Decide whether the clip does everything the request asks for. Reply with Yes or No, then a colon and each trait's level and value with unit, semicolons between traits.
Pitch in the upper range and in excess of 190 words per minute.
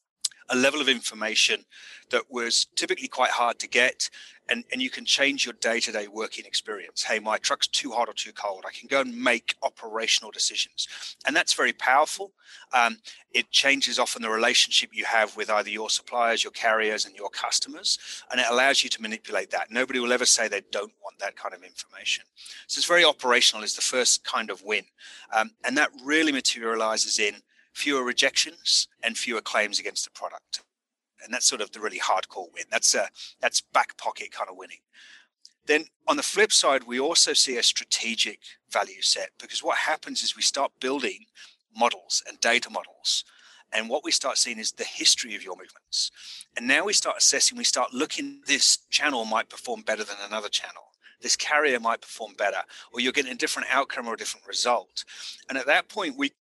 No: low, 135 Hz; average, 200 wpm